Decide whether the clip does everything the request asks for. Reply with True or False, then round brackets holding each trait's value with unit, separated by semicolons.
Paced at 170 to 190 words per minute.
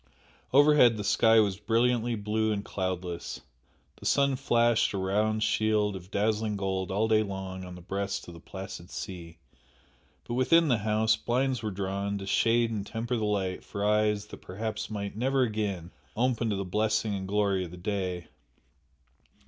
True (175 wpm)